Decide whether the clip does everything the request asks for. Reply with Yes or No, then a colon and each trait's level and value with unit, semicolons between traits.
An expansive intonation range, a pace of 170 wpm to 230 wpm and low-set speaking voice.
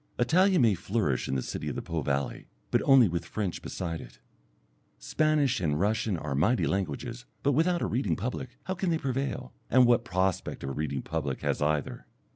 Yes: wide, 8.7 semitones; average, 195 wpm; low, 110 Hz